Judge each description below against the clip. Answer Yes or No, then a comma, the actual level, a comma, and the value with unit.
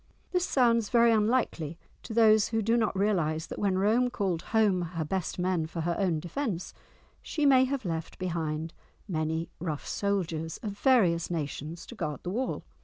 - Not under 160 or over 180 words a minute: Yes, average, 175 wpm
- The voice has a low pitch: No, medium, 185 Hz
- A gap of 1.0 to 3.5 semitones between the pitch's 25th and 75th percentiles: No, wide, 5.5 semitones